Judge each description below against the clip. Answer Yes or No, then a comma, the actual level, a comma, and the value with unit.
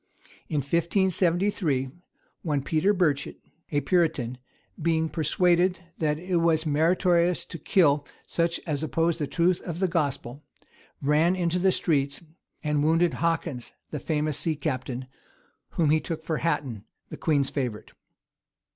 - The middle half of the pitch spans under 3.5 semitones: Yes, average, 2.9 semitones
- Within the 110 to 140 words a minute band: Yes, slow, 135 wpm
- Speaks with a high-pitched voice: No, medium, 160 Hz